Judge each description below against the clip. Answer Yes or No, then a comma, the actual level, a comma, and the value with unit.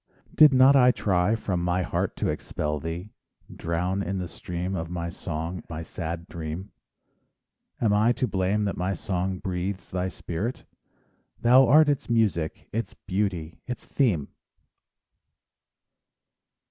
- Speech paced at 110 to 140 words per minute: Yes, slow, 135 wpm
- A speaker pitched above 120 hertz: No, very low, 95 Hz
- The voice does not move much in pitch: No, average, 4.1 semitones